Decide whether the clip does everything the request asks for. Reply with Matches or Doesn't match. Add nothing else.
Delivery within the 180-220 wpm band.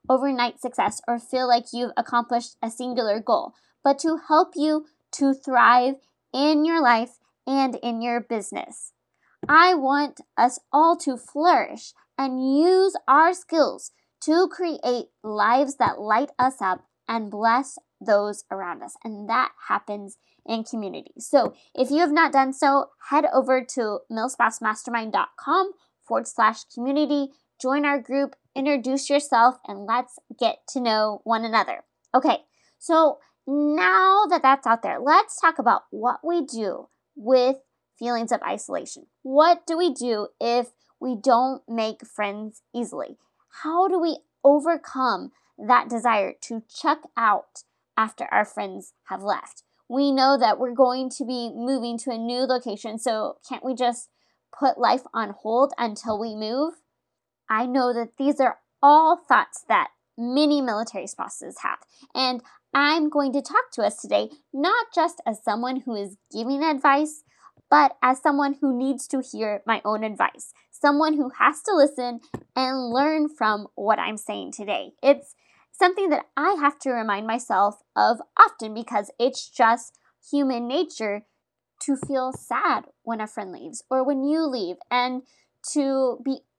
Doesn't match